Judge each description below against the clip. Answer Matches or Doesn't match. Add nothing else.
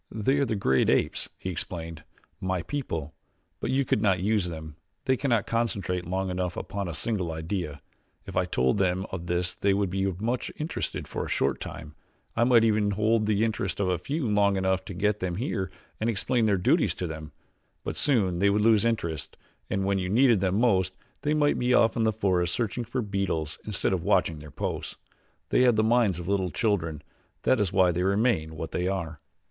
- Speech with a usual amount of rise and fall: Matches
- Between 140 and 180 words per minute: Doesn't match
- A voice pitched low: Matches